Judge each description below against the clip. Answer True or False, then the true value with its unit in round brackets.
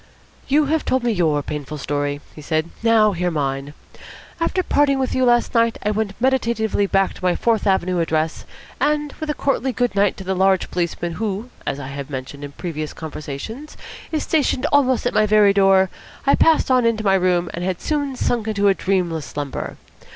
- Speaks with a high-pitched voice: True (195 Hz)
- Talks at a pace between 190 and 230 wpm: True (195 wpm)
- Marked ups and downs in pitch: True (6.9 semitones)